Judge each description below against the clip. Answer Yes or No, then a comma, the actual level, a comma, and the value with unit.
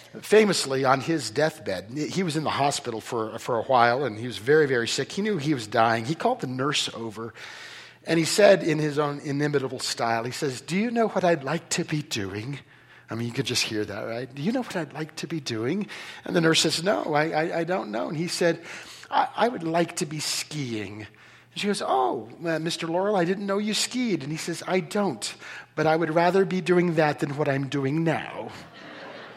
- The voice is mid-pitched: Yes, medium, 155 Hz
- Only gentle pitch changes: No, average, 4.5 semitones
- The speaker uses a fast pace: Yes, fast, 235 wpm